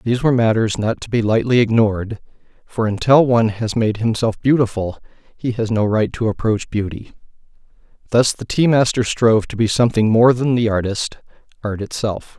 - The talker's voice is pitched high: No, low, 115 Hz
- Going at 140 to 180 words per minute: Yes, average, 170 wpm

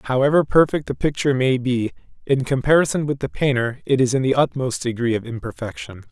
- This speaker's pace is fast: No, average, 185 wpm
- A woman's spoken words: No, male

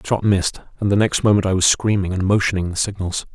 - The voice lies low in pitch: Yes, very low, 95 Hz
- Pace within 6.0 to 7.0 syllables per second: Yes, 6.5 syllables/s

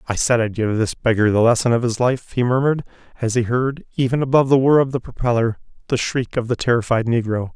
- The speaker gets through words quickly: Yes, fast, 230 wpm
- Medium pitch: No, low, 120 Hz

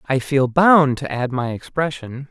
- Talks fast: No, average, 180 wpm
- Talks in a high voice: No, medium, 140 Hz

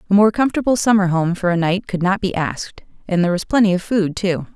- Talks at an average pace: No, fast, 250 wpm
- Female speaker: Yes, female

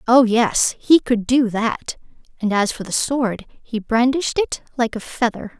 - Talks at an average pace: Yes, average, 180 wpm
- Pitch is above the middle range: Yes, high, 235 Hz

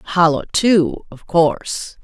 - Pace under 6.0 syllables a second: Yes, 3.3 syllables/s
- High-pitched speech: No, medium, 170 Hz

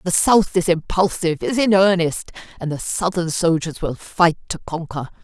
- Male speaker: No, female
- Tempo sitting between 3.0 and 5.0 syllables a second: Yes, 4.8 syllables/s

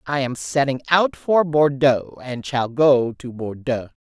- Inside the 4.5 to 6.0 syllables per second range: No, 3.8 syllables/s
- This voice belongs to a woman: Yes, female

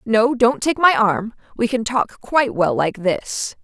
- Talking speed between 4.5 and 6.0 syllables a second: No, 4.0 syllables/s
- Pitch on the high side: Yes, high, 225 Hz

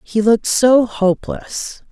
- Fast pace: No, slow, 125 wpm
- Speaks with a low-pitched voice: No, high, 225 Hz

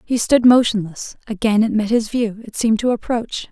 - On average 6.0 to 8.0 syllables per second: No, 5.2 syllables/s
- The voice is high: Yes, high, 220 Hz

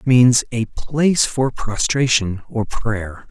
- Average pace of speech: Yes, average, 145 wpm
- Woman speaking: No, male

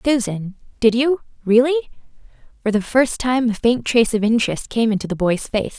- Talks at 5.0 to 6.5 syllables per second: Yes, 5.6 syllables/s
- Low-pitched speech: No, high, 230 Hz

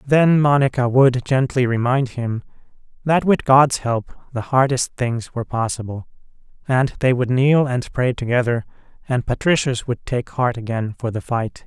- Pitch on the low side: Yes, low, 125 Hz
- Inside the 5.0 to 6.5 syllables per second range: No, 4.6 syllables/s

